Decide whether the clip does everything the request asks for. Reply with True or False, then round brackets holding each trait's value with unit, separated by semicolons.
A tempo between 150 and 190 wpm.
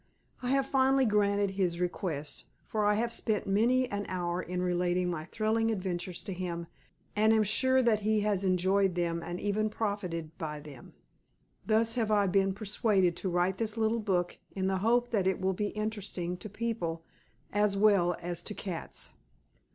True (175 wpm)